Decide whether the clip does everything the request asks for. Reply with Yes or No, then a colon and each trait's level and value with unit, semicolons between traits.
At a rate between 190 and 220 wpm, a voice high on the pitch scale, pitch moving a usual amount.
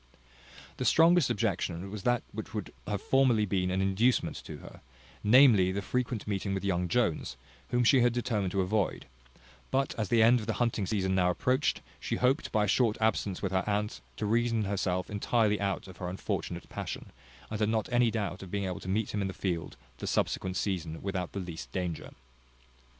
No: average, 200 wpm; low, 105 Hz; average, 3.7 semitones